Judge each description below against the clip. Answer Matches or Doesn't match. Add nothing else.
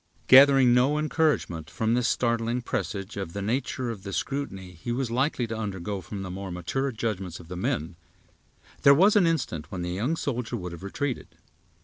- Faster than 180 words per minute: Matches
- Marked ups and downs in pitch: Matches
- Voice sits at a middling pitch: Doesn't match